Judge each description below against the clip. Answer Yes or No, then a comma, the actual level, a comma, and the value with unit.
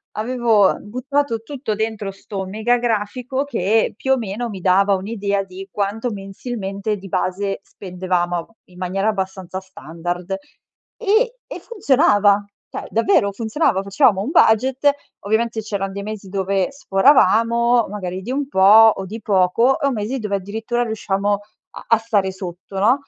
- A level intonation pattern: No, average, 3.5 semitones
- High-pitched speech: Yes, high, 205 Hz